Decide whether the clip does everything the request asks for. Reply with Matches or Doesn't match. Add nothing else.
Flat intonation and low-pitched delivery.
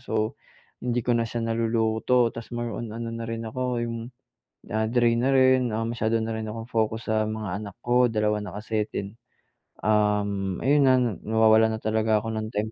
Matches